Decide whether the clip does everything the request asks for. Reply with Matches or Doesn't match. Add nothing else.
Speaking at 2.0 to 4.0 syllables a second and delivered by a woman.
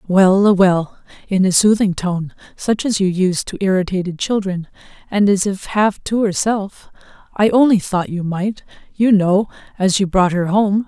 Matches